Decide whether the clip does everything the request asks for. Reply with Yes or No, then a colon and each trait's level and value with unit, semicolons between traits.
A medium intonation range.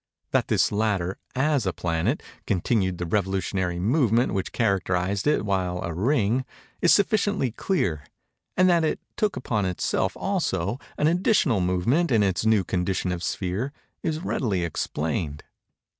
No: wide, 7.1 semitones